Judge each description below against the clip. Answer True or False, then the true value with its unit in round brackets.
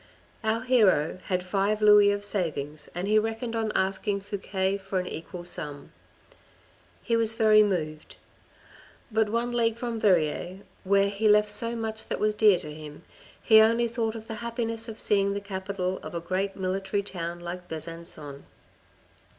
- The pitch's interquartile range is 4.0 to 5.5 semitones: False (3.4 semitones)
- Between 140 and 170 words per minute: True (165 wpm)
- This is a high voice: True (200 Hz)